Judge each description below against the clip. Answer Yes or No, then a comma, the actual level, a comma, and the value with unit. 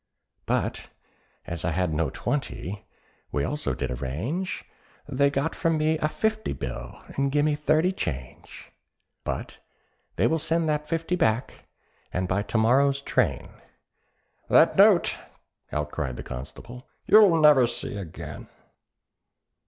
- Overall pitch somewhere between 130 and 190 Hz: Yes, low, 135 Hz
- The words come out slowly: Yes, slow, 130 wpm